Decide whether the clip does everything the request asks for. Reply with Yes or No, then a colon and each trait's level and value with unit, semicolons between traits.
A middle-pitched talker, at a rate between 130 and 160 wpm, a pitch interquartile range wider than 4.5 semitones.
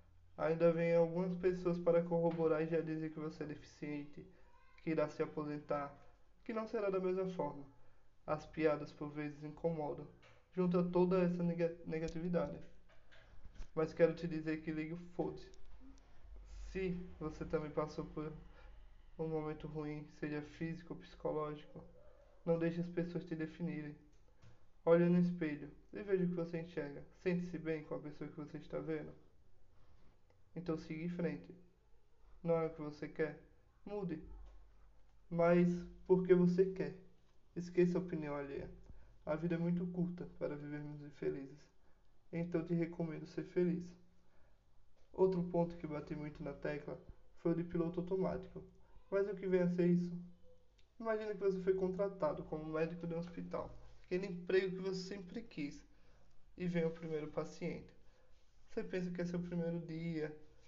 No: medium, 165 Hz; average, 155 wpm; average, 2.7 semitones